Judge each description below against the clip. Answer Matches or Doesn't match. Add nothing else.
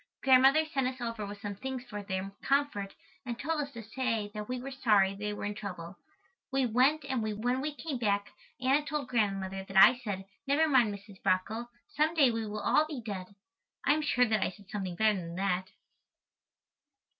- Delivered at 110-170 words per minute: Doesn't match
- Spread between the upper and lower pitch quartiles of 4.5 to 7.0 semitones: Matches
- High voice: Matches